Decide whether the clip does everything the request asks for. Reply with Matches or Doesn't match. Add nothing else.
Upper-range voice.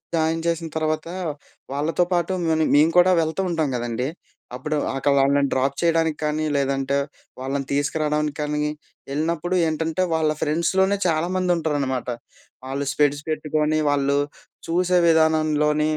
Doesn't match